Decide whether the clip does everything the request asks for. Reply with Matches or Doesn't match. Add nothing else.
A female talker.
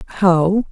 Matches